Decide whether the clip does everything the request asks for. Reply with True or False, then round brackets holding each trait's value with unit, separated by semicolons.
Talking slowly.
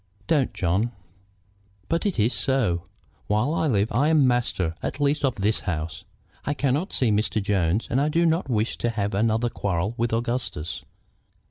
False (170 wpm)